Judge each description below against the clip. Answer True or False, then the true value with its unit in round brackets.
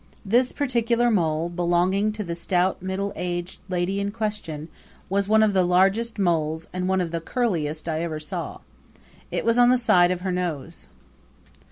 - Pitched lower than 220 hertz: True (185 Hz)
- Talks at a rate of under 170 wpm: False (175 wpm)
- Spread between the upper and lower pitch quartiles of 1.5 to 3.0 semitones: False (3.8 semitones)